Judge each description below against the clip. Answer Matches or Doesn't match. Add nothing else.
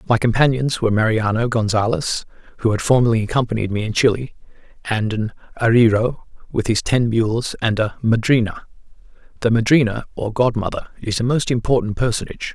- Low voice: Matches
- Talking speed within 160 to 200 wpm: Doesn't match